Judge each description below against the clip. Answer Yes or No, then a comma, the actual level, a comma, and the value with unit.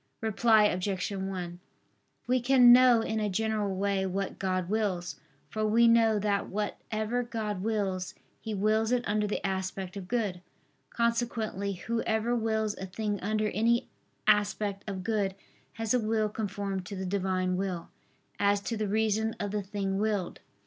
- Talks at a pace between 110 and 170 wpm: Yes, average, 155 wpm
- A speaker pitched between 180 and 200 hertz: No, high, 210 Hz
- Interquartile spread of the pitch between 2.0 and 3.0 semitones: Yes, narrow, 2.4 semitones